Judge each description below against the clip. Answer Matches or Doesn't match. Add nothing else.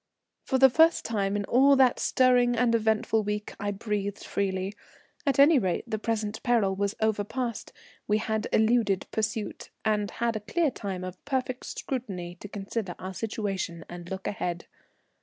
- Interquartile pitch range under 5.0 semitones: Matches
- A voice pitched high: Matches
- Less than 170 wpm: Matches